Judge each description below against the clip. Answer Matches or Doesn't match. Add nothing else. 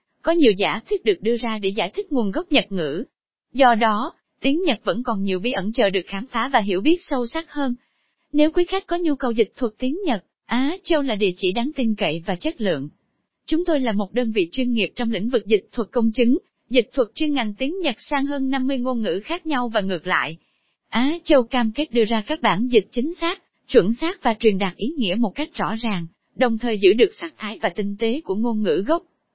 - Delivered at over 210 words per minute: Matches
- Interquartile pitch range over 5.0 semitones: Matches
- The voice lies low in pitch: Doesn't match